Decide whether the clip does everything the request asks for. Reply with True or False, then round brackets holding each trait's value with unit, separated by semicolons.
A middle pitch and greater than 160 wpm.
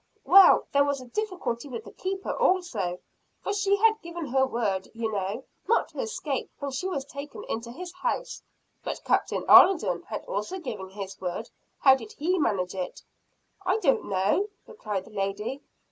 False (270 Hz; 175 wpm)